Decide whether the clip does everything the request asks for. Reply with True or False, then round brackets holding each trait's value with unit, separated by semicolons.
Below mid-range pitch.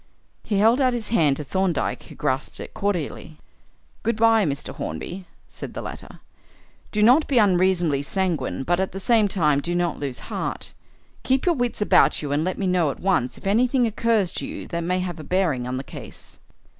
False (185 Hz)